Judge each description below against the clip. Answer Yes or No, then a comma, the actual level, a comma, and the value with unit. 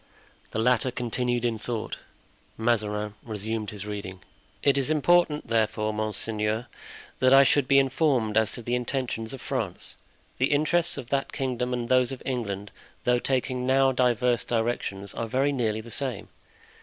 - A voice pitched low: Yes, low, 120 Hz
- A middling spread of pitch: Yes, average, 3.3 semitones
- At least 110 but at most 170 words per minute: Yes, average, 155 wpm